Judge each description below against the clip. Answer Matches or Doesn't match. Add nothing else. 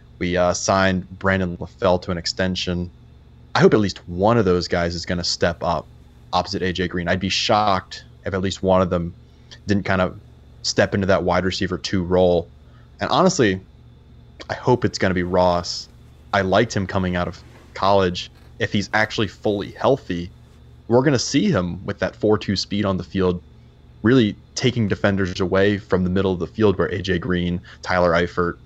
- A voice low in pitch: Matches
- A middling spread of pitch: Doesn't match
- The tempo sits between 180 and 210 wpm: Matches